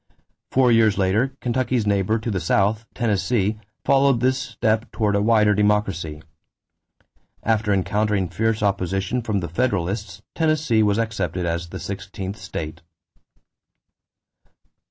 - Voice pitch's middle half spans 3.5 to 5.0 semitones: No, average, 3.1 semitones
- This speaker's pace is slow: Yes, slow, 120 wpm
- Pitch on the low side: Yes, low, 105 Hz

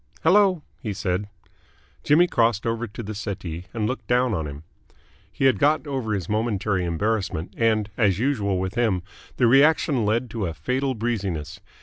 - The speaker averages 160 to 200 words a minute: Yes, average, 165 wpm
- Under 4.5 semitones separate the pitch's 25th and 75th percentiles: No, average, 4.8 semitones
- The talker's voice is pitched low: Yes, low, 110 Hz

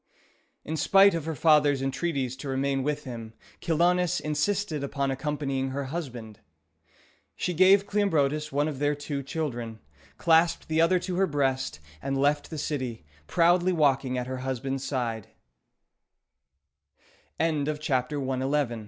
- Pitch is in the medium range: Yes, medium, 145 Hz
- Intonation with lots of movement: No, average, 3.7 semitones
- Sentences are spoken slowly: Yes, slow, 125 wpm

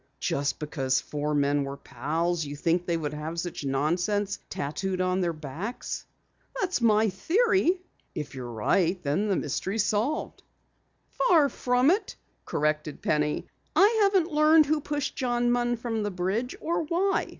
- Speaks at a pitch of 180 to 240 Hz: Yes, high, 190 Hz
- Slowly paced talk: No, average, 155 wpm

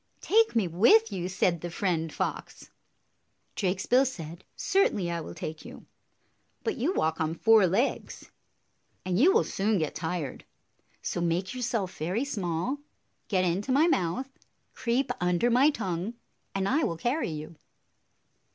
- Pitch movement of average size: No, wide, 6.2 semitones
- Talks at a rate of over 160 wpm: No, average, 145 wpm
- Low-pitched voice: No, high, 190 Hz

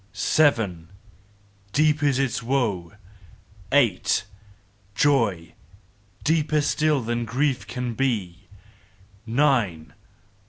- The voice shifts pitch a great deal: Yes, wide, 5.9 semitones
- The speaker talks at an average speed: No, slow, 80 wpm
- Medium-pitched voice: No, low, 125 Hz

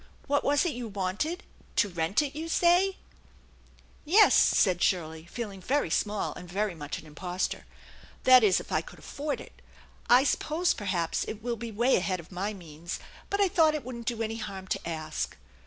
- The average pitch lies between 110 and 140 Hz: No, high, 215 Hz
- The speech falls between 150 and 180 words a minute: No, average, 195 wpm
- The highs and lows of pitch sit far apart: Yes, wide, 8.0 semitones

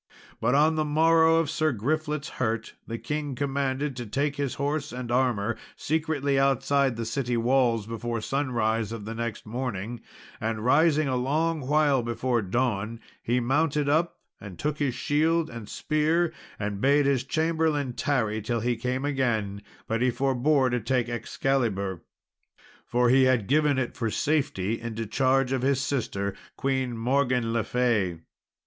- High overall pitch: No, low, 130 Hz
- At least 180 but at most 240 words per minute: No, average, 155 wpm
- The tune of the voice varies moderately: Yes, average, 3.9 semitones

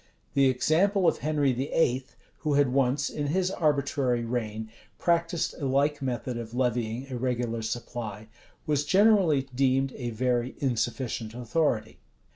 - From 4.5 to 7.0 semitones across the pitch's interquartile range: No, average, 3.5 semitones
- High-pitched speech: No, low, 130 Hz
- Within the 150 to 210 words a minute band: No, slow, 135 wpm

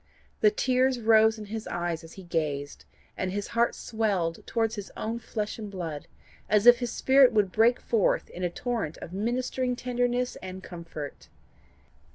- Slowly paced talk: No, average, 170 wpm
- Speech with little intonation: No, average, 4.9 semitones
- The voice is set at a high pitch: Yes, high, 220 Hz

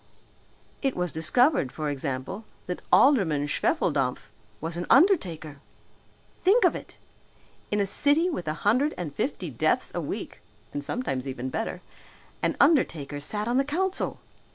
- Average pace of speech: Yes, average, 145 wpm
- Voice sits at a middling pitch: Yes, medium, 180 Hz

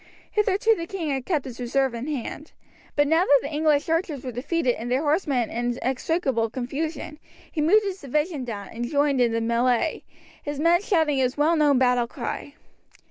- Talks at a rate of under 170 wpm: No, average, 190 wpm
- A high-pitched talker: Yes, very high, 285 Hz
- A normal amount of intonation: Yes, average, 4.5 semitones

